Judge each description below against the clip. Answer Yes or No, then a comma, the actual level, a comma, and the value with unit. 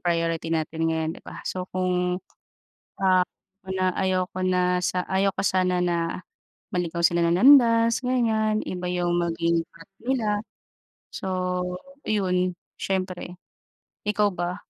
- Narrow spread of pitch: Yes, narrow, 2.0 semitones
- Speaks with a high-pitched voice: No, medium, 180 Hz